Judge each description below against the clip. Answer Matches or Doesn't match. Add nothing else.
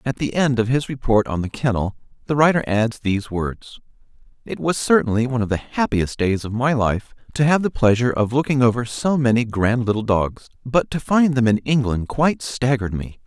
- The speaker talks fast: Matches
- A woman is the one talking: Doesn't match